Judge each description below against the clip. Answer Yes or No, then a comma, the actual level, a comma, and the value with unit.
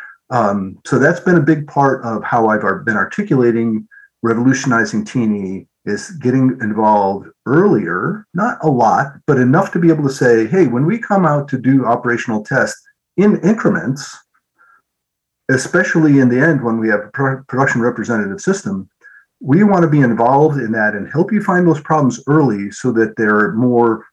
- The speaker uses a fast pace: No, average, 170 wpm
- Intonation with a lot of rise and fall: Yes, wide, 6.4 semitones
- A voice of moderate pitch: No, low, 130 Hz